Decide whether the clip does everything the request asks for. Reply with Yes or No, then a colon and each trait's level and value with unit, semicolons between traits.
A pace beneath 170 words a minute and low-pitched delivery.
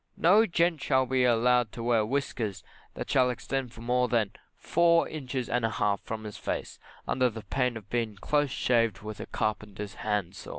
No: average, 185 wpm; low, 120 Hz